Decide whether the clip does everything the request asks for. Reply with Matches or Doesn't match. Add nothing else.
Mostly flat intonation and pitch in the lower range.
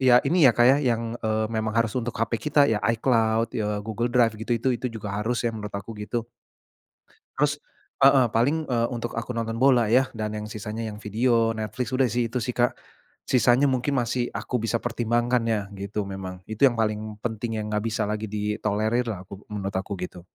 Matches